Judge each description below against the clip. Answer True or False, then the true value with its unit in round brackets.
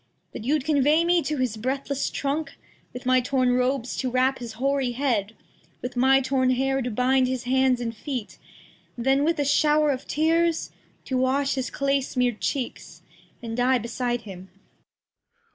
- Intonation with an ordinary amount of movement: False (2.1 semitones)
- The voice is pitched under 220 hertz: False (260 Hz)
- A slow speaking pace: False (165 wpm)